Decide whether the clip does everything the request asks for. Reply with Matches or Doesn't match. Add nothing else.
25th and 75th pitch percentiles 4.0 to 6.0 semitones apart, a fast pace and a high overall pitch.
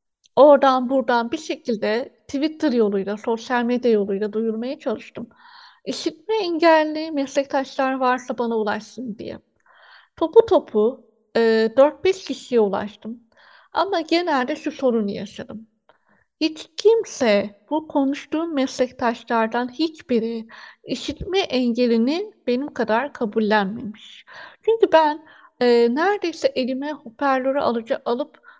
Doesn't match